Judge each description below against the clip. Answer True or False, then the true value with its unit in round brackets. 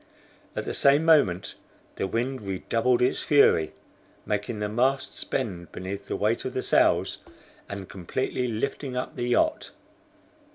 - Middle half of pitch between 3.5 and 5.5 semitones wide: True (4.6 semitones)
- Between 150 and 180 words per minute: False (140 wpm)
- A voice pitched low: True (115 Hz)